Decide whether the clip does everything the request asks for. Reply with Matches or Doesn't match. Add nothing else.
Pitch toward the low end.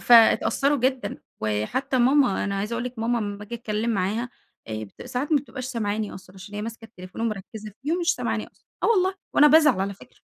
Doesn't match